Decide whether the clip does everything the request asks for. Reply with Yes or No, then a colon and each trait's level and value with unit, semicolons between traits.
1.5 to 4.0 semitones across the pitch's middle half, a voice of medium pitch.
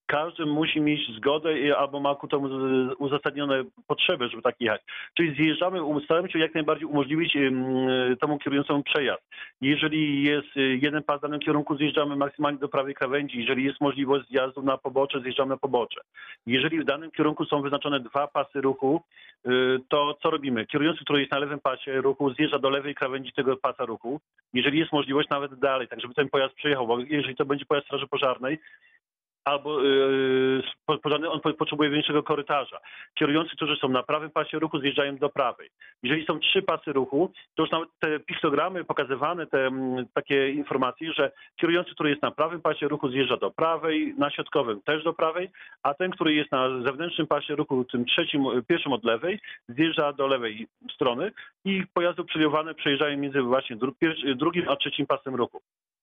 Yes: narrow, 2.4 semitones; medium, 145 Hz